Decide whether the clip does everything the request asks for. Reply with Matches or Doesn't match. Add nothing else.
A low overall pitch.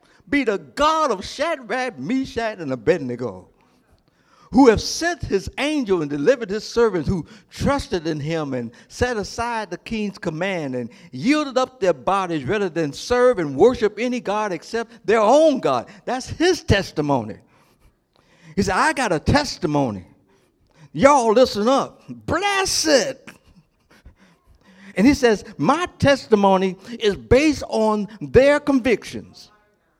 Doesn't match